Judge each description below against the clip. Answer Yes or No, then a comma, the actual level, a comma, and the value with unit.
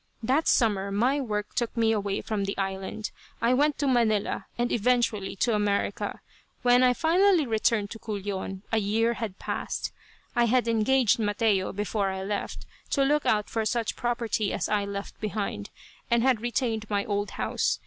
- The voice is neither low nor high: No, high, 220 Hz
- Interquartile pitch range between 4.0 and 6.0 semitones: No, average, 3.0 semitones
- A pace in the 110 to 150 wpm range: No, average, 170 wpm